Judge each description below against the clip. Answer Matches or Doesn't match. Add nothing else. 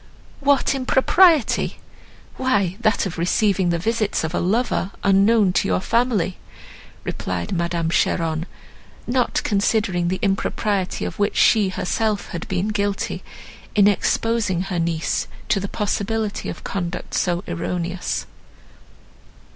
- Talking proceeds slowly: Matches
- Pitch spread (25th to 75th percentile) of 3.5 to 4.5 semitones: Matches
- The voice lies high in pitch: Matches